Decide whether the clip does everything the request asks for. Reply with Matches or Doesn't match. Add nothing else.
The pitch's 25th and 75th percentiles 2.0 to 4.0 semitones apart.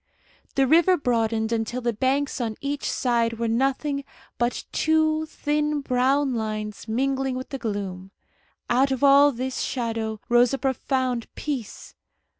Matches